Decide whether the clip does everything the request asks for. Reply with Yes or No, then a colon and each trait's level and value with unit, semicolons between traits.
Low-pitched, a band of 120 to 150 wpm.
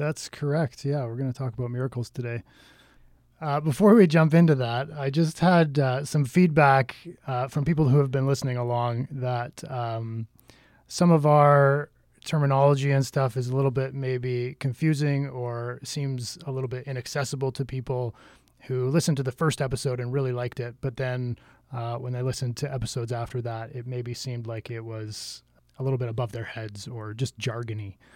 No: low, 130 Hz; average, 185 wpm